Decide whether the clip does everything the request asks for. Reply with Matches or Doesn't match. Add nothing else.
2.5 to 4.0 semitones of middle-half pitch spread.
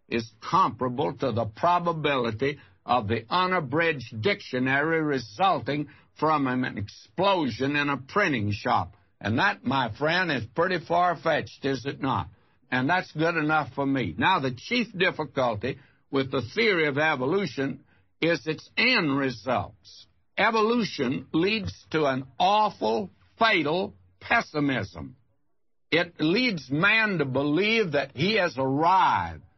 Doesn't match